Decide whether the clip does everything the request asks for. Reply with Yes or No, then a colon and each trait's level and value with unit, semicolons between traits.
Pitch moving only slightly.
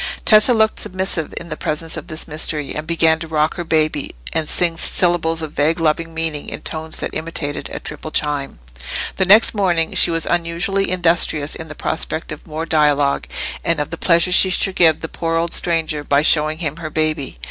Yes: narrow, 1.8 semitones